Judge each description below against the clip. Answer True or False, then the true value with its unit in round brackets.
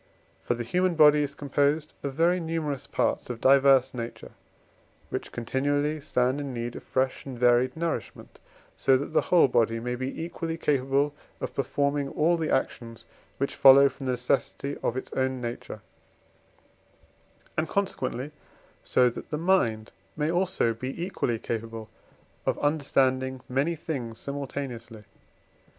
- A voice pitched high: False (135 Hz)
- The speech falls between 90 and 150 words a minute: True (145 wpm)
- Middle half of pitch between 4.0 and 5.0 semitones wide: False (3.4 semitones)